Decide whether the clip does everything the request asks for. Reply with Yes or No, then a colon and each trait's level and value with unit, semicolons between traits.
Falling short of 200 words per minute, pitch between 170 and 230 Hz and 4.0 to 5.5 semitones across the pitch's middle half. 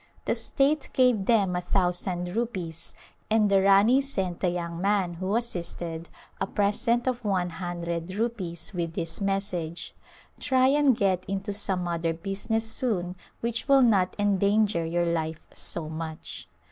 Yes: average, 150 wpm; high, 190 Hz; average, 4.4 semitones